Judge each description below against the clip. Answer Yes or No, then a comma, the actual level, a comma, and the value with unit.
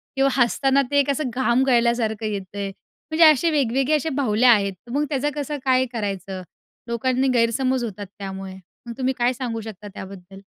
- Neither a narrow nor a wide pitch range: Yes, average, 4.4 semitones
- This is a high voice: Yes, high, 240 Hz